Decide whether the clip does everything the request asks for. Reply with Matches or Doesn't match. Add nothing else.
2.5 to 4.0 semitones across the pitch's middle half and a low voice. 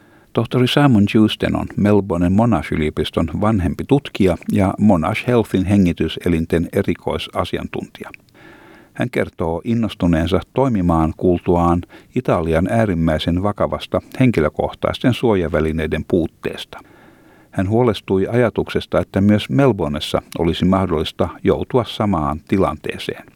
Doesn't match